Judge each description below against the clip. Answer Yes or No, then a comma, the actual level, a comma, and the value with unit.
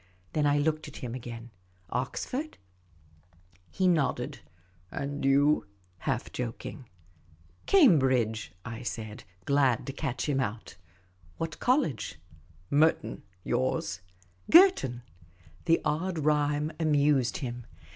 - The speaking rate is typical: No, slow, 125 wpm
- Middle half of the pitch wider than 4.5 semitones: Yes, wide, 5.4 semitones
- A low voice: Yes, low, 130 Hz